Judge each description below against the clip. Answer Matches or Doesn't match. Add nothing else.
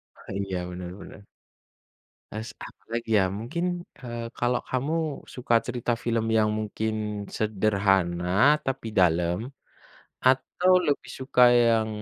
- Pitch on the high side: Doesn't match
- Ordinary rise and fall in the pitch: Matches